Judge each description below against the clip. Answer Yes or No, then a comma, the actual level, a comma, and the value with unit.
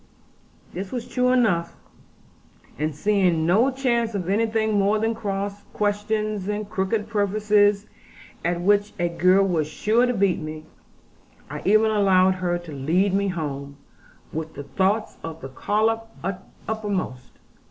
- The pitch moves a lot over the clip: No, average, 3.7 semitones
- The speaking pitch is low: No, high, 200 Hz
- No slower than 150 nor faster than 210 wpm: No, average, 140 wpm